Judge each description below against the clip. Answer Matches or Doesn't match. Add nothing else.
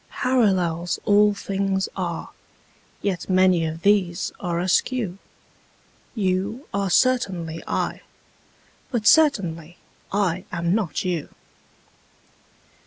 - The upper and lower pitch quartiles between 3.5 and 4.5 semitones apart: Doesn't match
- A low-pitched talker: Doesn't match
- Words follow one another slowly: Matches